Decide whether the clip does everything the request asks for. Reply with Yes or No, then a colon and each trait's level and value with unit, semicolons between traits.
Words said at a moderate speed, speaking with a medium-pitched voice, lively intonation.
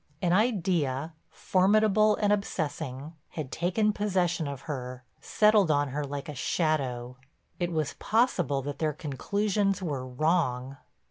No: slow, 130 wpm; medium, 160 Hz; wide, 6.1 semitones